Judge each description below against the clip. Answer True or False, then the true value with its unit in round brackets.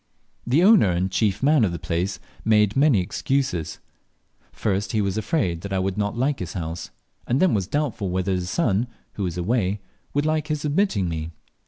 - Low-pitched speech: True (105 Hz)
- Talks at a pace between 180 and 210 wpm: True (185 wpm)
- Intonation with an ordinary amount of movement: False (6.9 semitones)